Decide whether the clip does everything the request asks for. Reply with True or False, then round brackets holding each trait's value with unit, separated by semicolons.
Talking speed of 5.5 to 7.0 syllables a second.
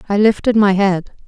False (5.0 syllables/s)